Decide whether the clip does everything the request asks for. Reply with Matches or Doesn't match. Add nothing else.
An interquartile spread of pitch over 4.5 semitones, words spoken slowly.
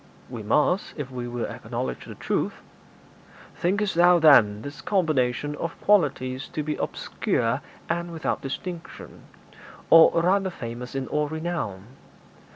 Matches